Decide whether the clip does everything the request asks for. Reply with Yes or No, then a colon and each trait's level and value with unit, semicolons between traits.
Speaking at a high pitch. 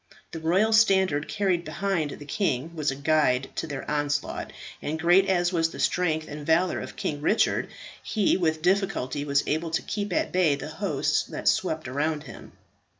No: medium, 160 Hz